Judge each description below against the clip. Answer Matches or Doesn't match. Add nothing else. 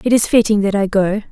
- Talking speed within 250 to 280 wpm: Matches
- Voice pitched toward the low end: Doesn't match